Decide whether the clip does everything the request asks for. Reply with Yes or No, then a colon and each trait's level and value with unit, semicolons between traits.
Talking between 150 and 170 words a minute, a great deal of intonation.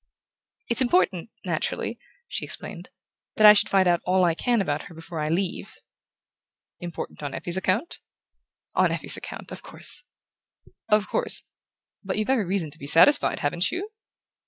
No: average, 155 wpm; average, 4.1 semitones